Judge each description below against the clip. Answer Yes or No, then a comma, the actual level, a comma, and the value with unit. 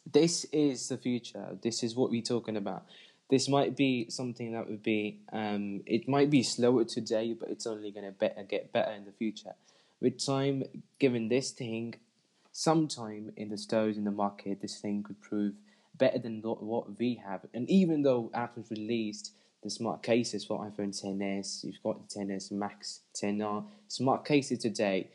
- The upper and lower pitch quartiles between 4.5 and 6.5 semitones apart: No, average, 3.4 semitones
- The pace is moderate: Yes, average, 180 wpm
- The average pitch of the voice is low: Yes, low, 115 Hz